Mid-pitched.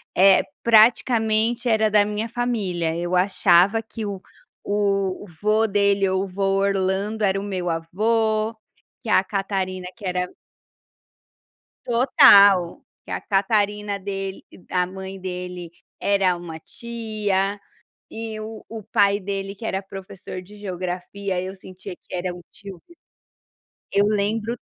No: high, 200 Hz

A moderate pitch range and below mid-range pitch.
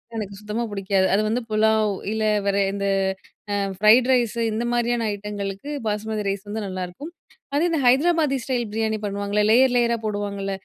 No: average, 3.0 semitones; high, 215 Hz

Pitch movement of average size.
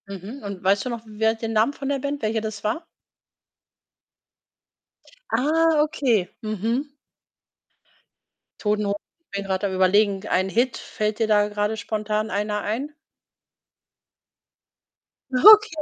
Yes: average, 3.6 semitones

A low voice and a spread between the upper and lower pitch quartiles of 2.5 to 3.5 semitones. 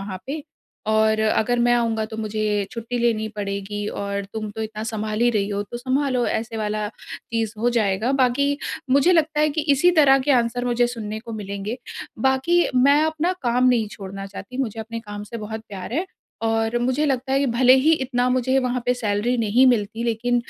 No: high, 235 Hz; average, 3.1 semitones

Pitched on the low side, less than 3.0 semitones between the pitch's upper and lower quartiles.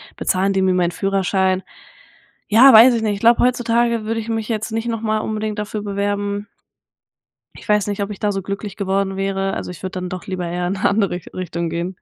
No: high, 200 Hz; narrow, 2.4 semitones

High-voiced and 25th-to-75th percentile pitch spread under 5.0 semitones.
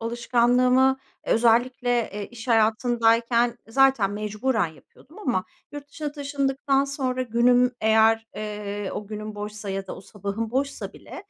Yes: high, 235 Hz; average, 3.4 semitones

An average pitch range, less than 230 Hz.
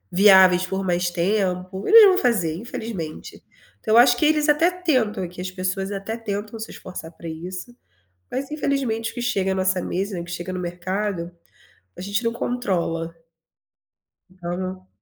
Yes: average, 4.3 semitones; high, 190 Hz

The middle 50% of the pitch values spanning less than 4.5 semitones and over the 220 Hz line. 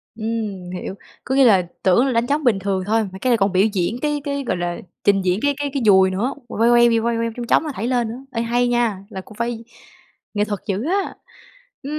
Yes: average, 4.0 semitones; high, 230 Hz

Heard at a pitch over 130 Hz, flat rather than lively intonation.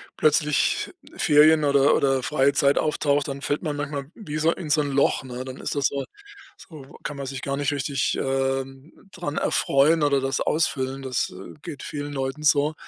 Yes: medium, 140 Hz; narrow, 1.8 semitones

